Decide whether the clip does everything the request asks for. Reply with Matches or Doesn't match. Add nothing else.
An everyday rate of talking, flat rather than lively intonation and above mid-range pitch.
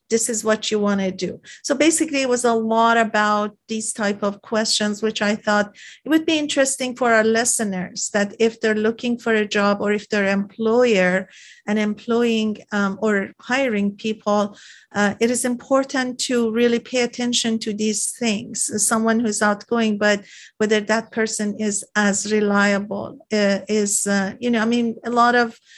Matches